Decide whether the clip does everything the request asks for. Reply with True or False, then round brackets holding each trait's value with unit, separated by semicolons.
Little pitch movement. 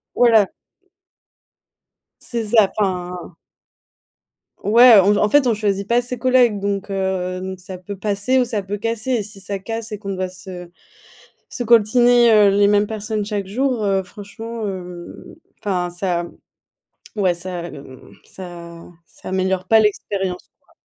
False (3.1 semitones)